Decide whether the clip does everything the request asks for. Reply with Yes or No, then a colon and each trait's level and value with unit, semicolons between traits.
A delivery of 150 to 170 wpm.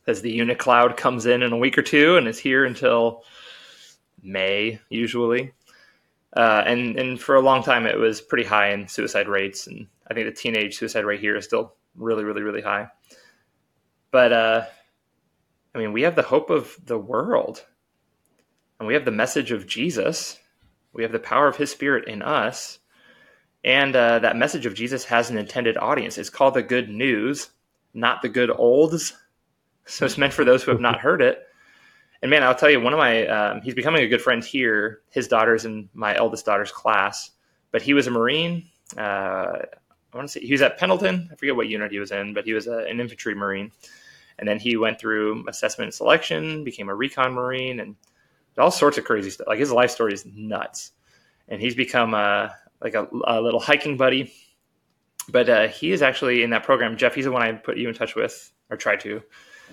No: fast, 205 wpm